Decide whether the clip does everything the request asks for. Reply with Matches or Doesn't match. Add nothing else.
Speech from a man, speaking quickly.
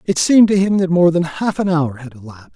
Matches